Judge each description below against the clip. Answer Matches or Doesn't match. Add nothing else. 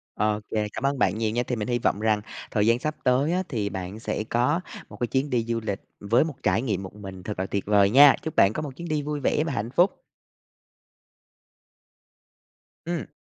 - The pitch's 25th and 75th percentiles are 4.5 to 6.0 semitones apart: Matches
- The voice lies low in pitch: Matches